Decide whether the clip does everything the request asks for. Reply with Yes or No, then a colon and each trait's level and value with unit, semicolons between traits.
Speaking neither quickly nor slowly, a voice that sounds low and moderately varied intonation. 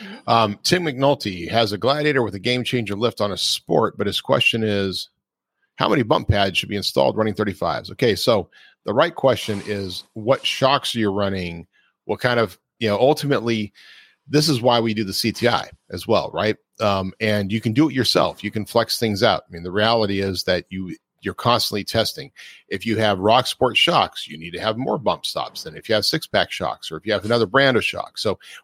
No: fast, 220 wpm; low, 110 Hz; average, 3.1 semitones